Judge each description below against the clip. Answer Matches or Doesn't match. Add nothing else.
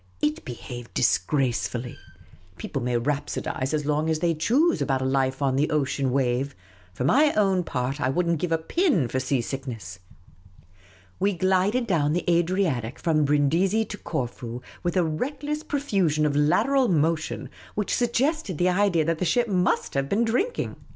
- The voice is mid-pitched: Matches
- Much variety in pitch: Matches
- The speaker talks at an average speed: Matches